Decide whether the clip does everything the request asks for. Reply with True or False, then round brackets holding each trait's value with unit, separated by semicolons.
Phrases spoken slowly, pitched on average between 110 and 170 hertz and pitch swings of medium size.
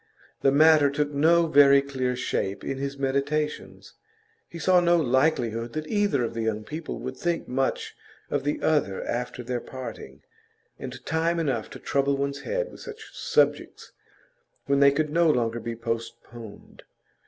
False (160 wpm; 140 Hz; 4.1 semitones)